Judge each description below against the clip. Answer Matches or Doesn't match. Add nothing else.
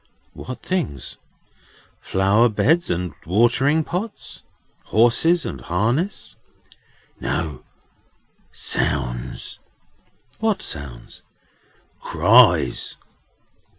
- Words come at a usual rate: Doesn't match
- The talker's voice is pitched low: Matches